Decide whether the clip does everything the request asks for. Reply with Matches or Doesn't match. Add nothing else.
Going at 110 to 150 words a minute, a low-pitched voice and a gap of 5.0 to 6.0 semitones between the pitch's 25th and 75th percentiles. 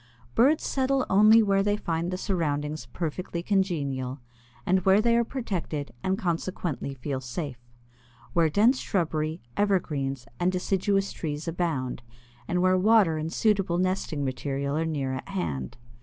Doesn't match